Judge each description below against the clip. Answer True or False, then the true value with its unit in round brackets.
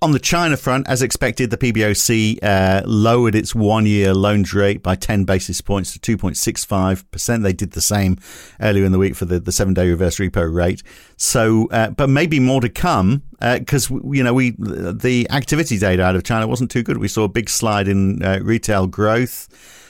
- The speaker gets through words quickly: False (195 wpm)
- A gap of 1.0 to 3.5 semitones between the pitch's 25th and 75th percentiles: False (4.2 semitones)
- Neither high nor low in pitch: False (105 Hz)